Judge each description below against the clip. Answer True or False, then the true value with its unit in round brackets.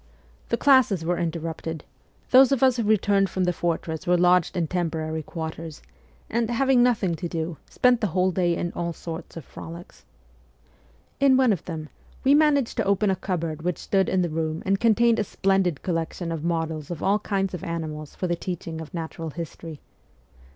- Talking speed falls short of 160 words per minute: False (185 wpm)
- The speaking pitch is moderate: True (175 Hz)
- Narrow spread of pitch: False (3.8 semitones)